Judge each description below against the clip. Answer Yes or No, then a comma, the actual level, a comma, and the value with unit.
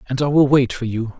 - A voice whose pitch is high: No, low, 130 Hz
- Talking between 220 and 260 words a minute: No, fast, 300 wpm